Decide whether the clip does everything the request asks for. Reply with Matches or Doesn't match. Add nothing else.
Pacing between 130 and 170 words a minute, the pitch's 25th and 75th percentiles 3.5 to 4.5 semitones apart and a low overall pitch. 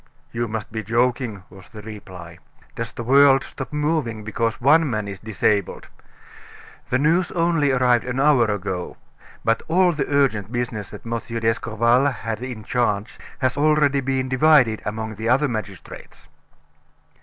Matches